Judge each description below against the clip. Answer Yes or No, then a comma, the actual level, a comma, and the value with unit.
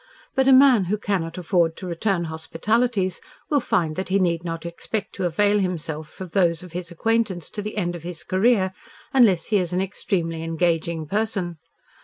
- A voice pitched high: No, medium, 180 Hz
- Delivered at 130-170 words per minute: No, average, 185 wpm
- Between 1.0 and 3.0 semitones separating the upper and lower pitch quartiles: No, average, 3.7 semitones